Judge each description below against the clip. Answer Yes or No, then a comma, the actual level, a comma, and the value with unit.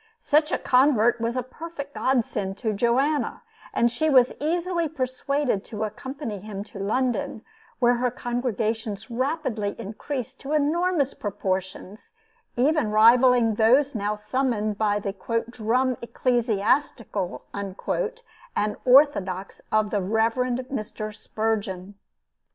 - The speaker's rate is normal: No, slow, 115 wpm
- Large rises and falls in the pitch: No, average, 4.2 semitones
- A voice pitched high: Yes, high, 235 Hz